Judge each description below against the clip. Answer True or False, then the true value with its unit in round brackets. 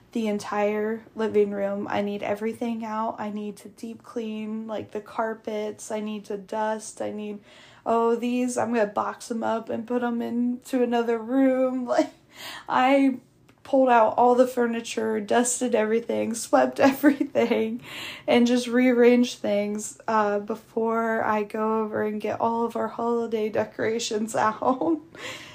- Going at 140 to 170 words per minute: True (145 wpm)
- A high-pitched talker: True (225 Hz)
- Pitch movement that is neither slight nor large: False (2.1 semitones)